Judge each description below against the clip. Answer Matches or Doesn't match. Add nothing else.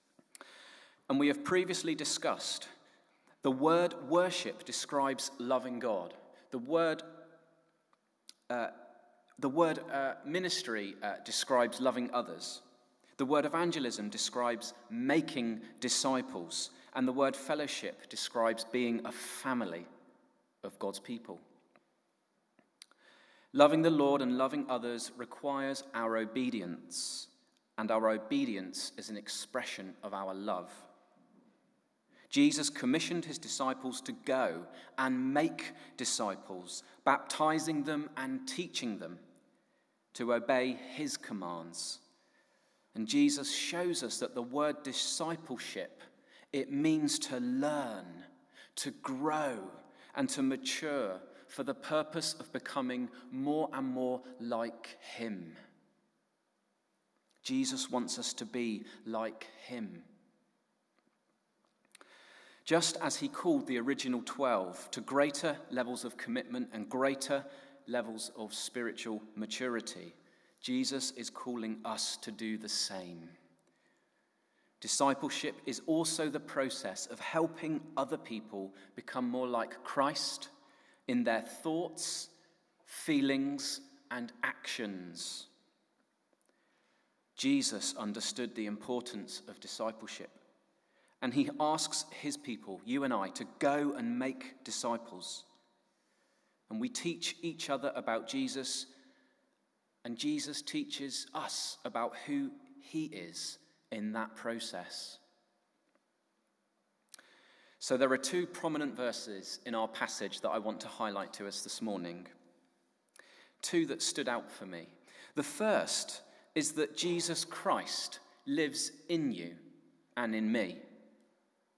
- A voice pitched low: Doesn't match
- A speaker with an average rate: Doesn't match